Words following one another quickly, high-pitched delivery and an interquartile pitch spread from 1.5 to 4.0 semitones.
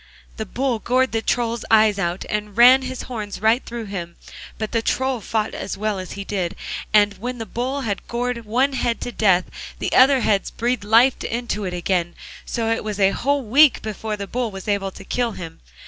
Yes: fast, 210 wpm; high, 220 Hz; average, 3.4 semitones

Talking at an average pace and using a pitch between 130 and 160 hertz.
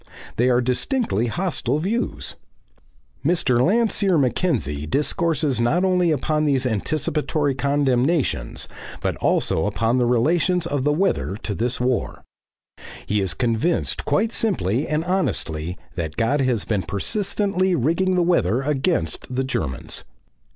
No: slow, 130 wpm; low, 135 Hz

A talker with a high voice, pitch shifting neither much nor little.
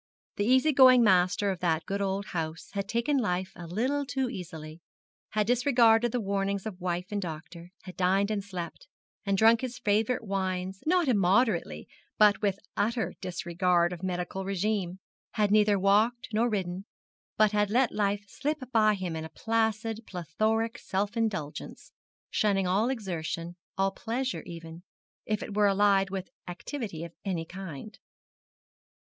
Yes: high, 200 Hz; average, 3.7 semitones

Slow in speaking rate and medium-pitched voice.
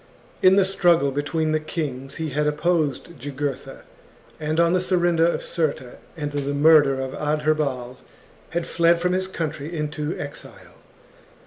No: average, 145 wpm; medium, 155 Hz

